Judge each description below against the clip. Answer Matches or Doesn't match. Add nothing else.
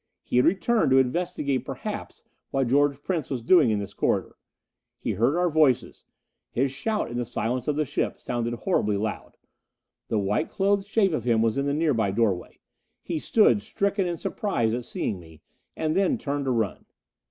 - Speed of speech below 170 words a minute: Doesn't match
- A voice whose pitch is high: Doesn't match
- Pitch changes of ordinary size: Doesn't match